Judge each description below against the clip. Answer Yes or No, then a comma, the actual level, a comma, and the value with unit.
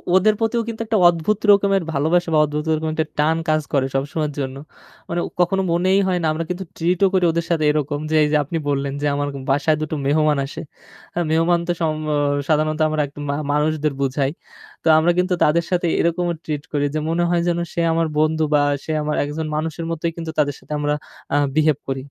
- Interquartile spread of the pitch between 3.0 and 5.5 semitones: No, narrow, 2.6 semitones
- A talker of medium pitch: Yes, medium, 155 Hz